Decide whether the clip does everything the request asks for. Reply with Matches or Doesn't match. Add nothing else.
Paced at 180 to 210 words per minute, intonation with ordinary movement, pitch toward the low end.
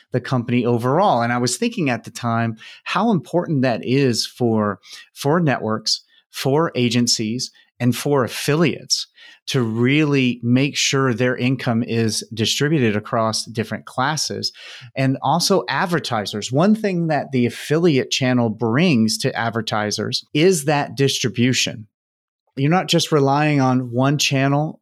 Doesn't match